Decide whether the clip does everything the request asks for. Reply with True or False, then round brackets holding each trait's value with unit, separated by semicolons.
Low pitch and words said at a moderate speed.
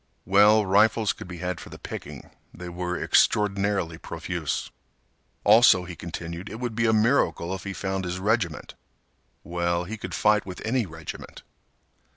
True (95 Hz; 160 wpm)